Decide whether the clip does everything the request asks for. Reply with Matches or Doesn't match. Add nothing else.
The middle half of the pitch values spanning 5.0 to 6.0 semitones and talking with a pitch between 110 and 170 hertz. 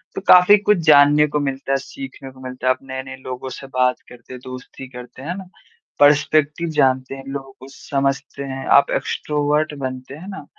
Doesn't match